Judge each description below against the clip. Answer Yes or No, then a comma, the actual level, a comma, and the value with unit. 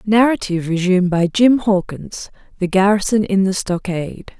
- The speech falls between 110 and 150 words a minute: Yes, slow, 135 wpm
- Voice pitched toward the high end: Yes, high, 195 Hz